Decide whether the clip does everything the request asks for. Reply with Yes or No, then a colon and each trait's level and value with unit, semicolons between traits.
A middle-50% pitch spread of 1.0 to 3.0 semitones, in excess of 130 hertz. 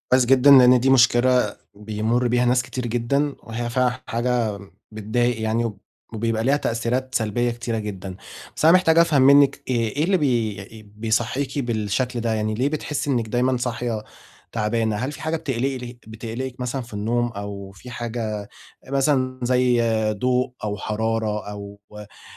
No: average, 2.7 semitones; low, 120 Hz